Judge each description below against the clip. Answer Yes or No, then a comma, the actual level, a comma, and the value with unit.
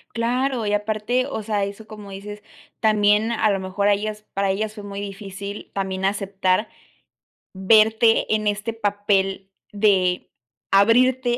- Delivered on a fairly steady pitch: Yes, narrow, 1.8 semitones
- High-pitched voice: Yes, high, 205 Hz